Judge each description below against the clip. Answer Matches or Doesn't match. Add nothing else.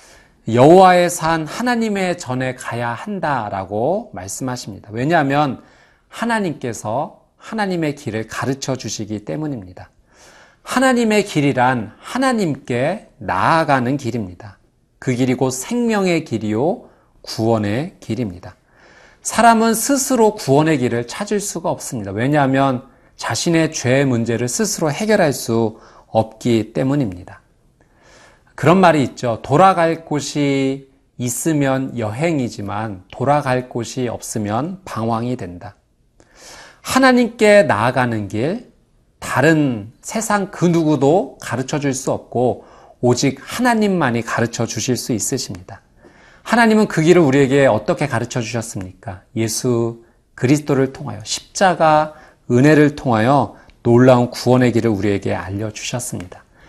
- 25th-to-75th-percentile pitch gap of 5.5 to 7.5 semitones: Matches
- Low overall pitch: Matches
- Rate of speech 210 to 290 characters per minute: Matches